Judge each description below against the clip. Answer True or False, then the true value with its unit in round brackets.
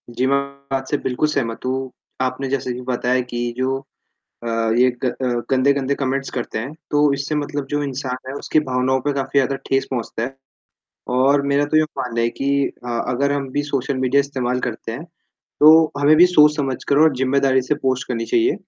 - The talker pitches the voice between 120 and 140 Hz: True (135 Hz)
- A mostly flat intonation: True (2.0 semitones)